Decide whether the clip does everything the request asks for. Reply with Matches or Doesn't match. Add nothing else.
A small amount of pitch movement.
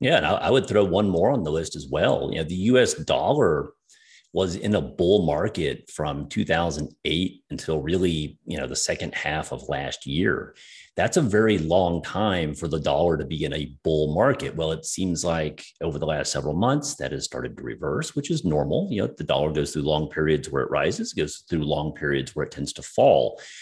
Doesn't match